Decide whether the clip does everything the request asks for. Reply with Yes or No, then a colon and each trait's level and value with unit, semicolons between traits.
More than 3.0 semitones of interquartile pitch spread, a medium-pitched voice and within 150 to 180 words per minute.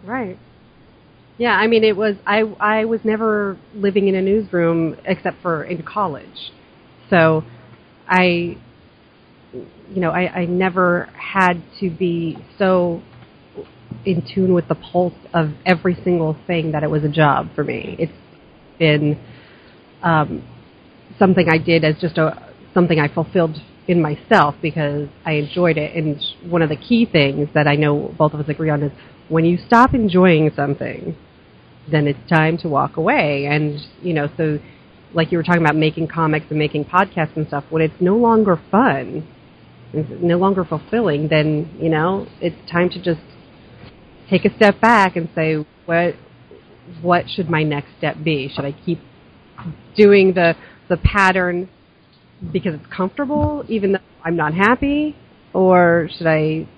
Yes: average, 3.5 semitones; medium, 170 Hz; average, 160 wpm